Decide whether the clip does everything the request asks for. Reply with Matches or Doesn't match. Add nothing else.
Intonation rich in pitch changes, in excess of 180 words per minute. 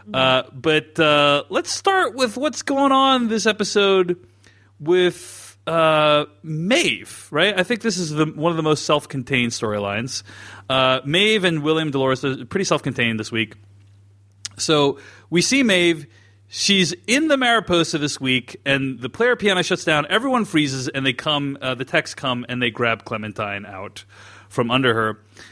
Doesn't match